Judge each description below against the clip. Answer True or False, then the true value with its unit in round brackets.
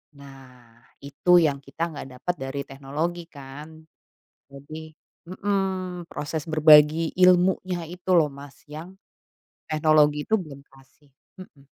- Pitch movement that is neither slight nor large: True (3.8 semitones)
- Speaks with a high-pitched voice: False (155 Hz)